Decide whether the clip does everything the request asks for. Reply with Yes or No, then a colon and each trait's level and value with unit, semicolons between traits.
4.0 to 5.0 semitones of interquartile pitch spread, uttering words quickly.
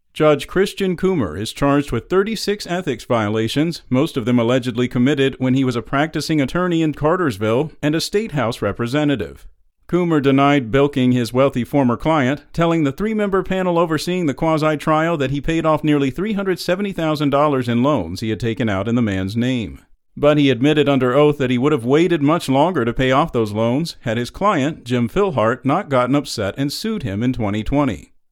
No: average, 4.6 semitones; average, 185 wpm